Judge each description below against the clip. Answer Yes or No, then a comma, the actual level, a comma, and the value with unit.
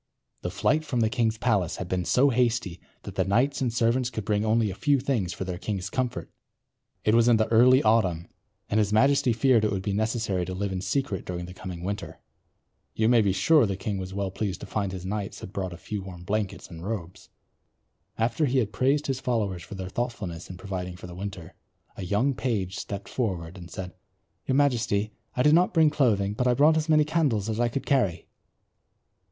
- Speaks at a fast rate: Yes, fast, 215 wpm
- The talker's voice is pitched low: Yes, low, 105 Hz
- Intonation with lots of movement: No, average, 4.8 semitones